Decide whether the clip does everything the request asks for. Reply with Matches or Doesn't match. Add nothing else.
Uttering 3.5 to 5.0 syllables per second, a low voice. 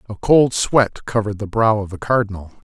Doesn't match